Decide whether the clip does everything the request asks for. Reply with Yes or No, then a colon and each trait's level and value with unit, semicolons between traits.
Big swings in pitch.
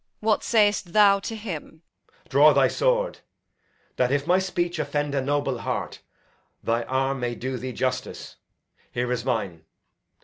Yes: wide, 6.9 semitones